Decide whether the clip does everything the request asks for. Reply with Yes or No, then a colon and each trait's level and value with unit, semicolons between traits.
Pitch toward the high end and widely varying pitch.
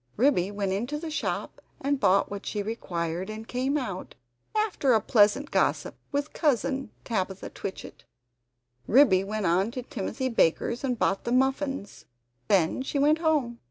Yes: high, 235 Hz; wide, 5.7 semitones